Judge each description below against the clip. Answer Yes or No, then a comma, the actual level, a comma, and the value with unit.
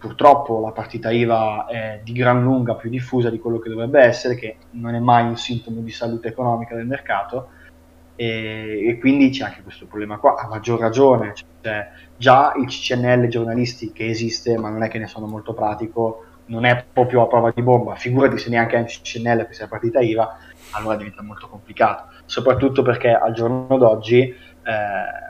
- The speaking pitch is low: Yes, low, 115 Hz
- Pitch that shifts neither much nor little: No, narrow, 1.9 semitones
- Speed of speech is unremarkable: No, fast, 185 wpm